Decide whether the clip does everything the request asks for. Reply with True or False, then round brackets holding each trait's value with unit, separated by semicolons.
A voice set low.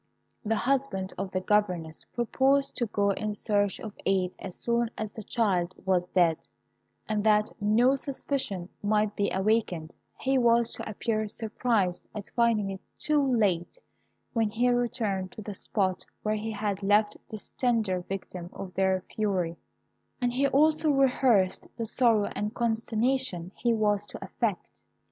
False (210 Hz)